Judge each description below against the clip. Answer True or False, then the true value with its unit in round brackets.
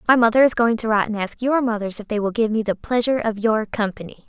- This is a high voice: True (225 Hz)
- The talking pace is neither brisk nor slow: False (280 wpm)